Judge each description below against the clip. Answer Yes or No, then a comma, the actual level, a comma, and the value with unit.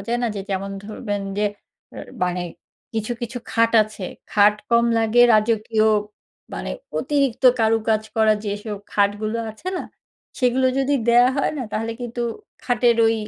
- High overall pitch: Yes, high, 225 Hz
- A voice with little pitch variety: Yes, narrow, 2.3 semitones